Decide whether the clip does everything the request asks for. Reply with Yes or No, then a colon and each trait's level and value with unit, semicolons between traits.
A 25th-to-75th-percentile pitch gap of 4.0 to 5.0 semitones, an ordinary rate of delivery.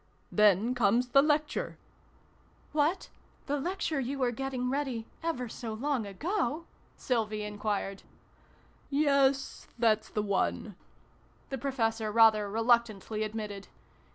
No: average, 4.5 semitones; slow, 125 wpm